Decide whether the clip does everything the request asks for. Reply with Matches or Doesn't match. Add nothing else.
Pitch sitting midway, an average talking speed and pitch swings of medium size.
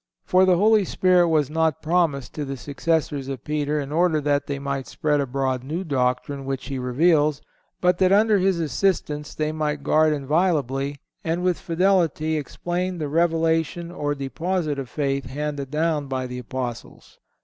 Matches